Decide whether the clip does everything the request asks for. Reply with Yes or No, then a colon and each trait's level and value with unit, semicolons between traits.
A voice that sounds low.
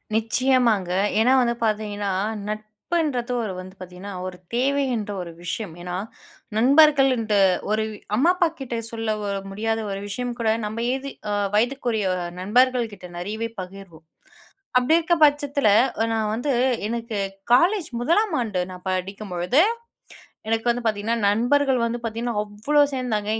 No: high, 225 Hz